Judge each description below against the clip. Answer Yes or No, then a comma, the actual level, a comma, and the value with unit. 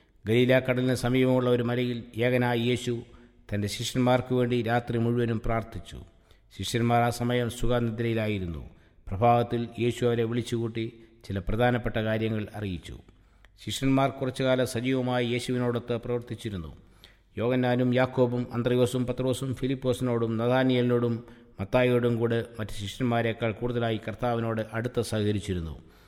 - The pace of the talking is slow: Yes, slow, 95 wpm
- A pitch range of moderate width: No, narrow, 1.9 semitones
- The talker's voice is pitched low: Yes, low, 120 Hz